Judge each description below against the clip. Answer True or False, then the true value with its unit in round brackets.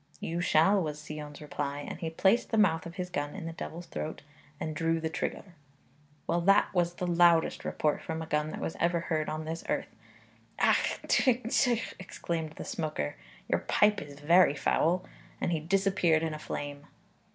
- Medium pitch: True (165 Hz)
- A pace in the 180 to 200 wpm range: True (185 wpm)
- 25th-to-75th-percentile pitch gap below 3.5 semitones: True (2.7 semitones)